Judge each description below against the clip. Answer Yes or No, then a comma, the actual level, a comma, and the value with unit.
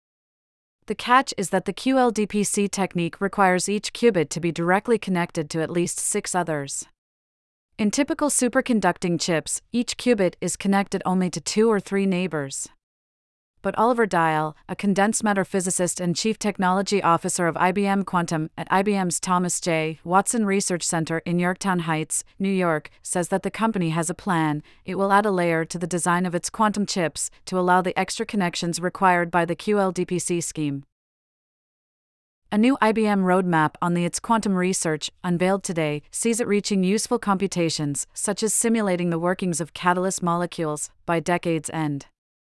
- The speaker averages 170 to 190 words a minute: No, average, 160 wpm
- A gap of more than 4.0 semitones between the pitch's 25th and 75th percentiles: No, average, 3.0 semitones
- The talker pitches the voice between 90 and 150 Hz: No, medium, 180 Hz